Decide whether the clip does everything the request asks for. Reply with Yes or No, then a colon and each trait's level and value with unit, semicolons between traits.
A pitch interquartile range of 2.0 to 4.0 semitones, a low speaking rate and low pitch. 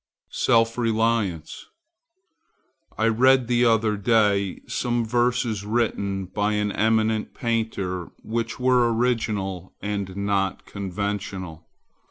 Yes: average, 2.8 semitones; slow, 100 wpm; low, 110 Hz